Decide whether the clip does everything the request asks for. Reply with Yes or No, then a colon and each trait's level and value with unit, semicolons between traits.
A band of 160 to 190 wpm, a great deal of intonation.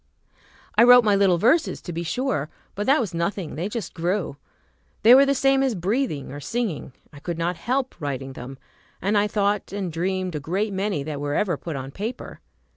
No: average, 200 wpm; wide, 5.9 semitones